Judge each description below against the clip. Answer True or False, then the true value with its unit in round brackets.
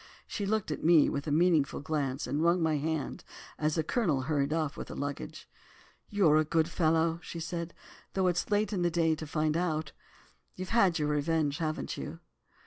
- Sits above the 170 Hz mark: False (160 Hz)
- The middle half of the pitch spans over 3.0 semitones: False (2.4 semitones)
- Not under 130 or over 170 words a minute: False (200 wpm)